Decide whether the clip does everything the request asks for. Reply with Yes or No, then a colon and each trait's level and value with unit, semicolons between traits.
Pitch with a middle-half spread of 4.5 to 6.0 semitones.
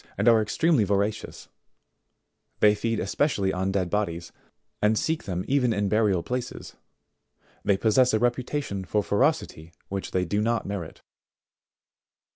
No: average, 3.8 semitones